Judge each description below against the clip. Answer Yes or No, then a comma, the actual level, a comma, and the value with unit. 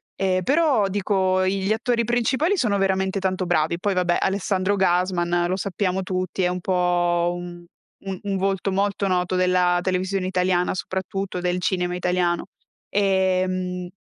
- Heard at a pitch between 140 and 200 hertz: Yes, medium, 185 Hz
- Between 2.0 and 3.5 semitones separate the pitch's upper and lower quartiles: No, narrow, 1.5 semitones